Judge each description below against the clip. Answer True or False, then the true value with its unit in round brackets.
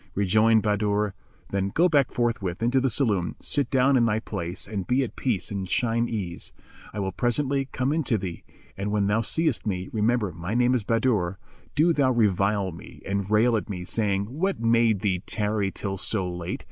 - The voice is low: True (110 Hz)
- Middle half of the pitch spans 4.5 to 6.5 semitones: False (3.8 semitones)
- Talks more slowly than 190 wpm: False (195 wpm)